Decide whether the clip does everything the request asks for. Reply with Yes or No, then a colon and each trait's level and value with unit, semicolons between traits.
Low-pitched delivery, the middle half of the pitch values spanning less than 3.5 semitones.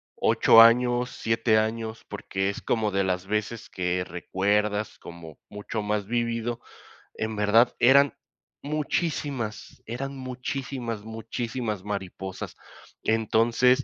Yes: low, 110 Hz; average, 2.9 semitones